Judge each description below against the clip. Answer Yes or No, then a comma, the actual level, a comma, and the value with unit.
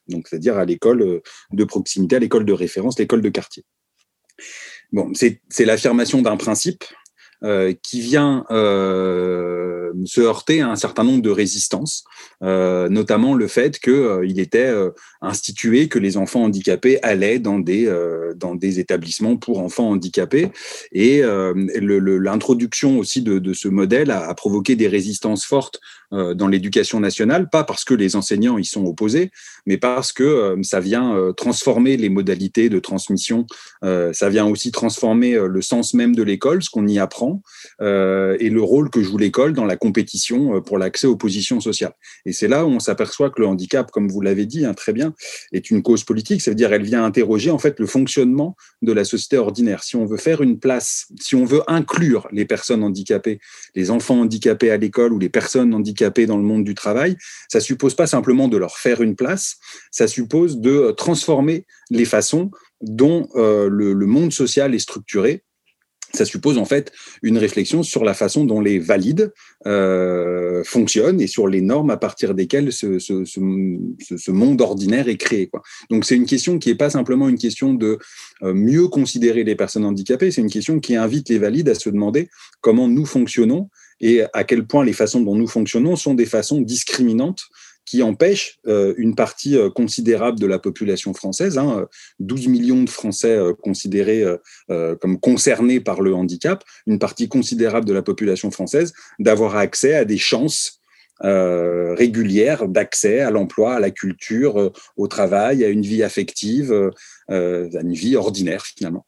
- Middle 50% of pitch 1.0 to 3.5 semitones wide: No, average, 5.2 semitones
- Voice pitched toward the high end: No, low, 110 Hz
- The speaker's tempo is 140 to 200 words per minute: Yes, average, 175 wpm